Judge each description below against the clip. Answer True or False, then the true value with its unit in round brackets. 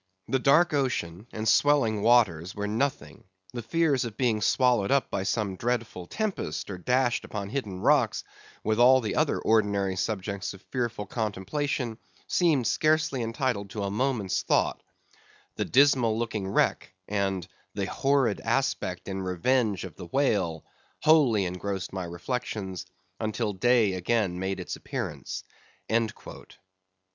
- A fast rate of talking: False (135 wpm)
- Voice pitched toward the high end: False (110 Hz)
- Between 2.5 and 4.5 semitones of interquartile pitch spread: False (4.9 semitones)